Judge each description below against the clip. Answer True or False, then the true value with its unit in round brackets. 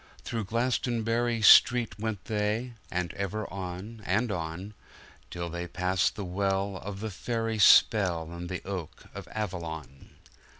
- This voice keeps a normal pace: False (130 wpm)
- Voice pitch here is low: True (100 Hz)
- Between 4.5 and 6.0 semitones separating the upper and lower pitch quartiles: False (3.9 semitones)